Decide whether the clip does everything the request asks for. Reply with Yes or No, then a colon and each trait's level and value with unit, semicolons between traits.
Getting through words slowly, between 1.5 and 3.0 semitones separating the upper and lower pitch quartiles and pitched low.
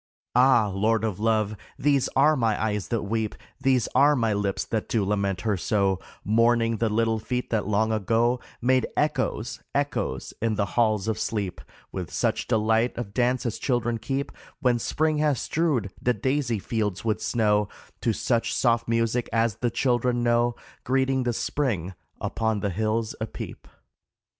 No: average, 165 wpm; narrow, 2.6 semitones; low, 115 Hz